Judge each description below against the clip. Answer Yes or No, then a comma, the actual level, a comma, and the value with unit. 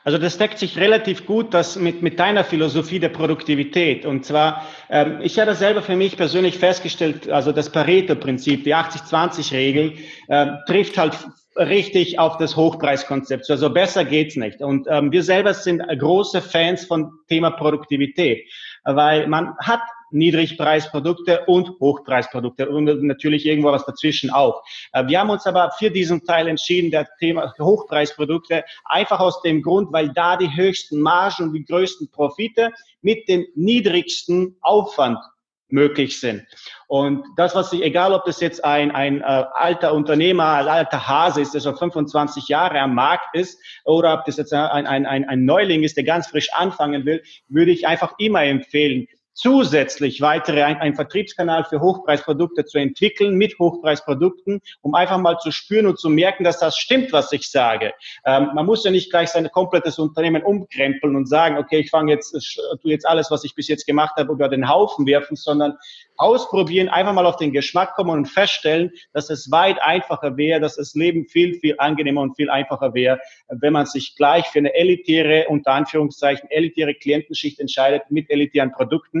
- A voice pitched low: No, medium, 155 Hz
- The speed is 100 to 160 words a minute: No, average, 175 wpm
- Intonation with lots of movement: No, average, 3.5 semitones